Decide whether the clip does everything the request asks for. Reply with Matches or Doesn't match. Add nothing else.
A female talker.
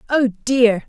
Matches